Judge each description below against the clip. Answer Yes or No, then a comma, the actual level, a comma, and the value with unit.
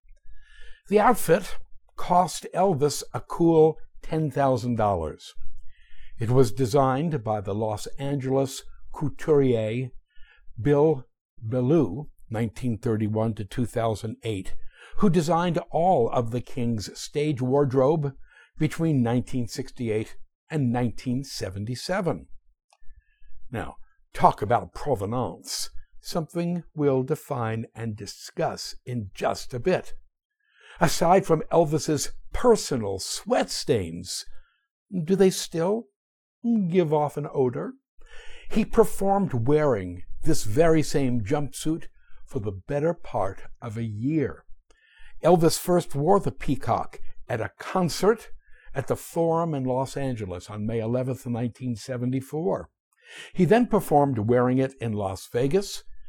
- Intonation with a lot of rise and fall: Yes, wide, 6.4 semitones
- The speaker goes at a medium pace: No, slow, 105 wpm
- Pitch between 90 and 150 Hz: Yes, medium, 140 Hz